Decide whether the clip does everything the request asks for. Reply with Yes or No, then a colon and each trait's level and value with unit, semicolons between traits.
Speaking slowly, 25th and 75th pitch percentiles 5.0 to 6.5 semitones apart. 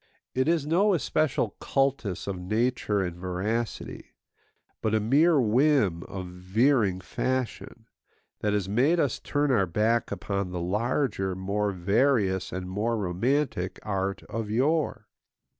Yes: slow, 130 wpm; wide, 5.6 semitones